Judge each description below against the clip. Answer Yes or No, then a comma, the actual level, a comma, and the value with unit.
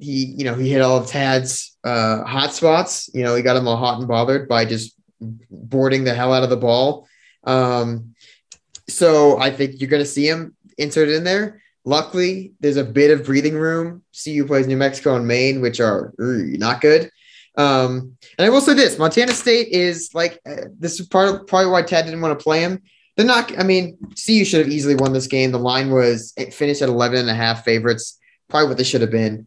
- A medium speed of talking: No, fast, 225 wpm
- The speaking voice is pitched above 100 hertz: Yes, medium, 140 Hz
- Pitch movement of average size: Yes, average, 4.6 semitones